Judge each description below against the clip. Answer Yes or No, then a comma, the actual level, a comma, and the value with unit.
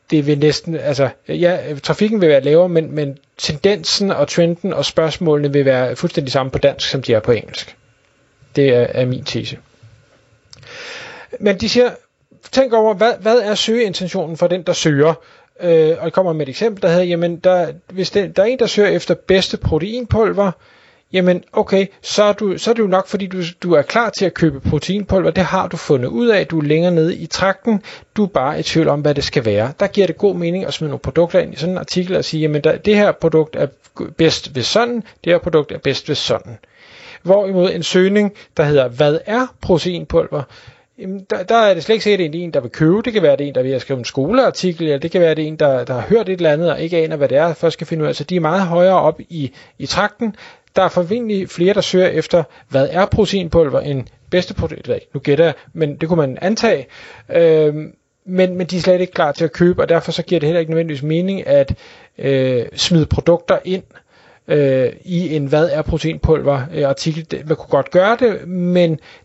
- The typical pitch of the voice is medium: Yes, medium, 170 Hz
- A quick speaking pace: Yes, fast, 235 wpm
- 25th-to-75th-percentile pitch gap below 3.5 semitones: No, average, 4.3 semitones